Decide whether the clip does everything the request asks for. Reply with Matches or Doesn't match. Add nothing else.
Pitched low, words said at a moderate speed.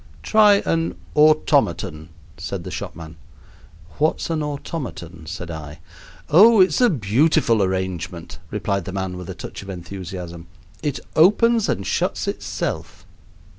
Doesn't match